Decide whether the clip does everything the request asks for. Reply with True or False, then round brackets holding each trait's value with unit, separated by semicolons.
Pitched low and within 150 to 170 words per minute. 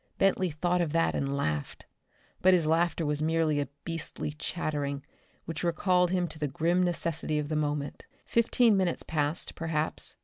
False (160 Hz; 165 wpm)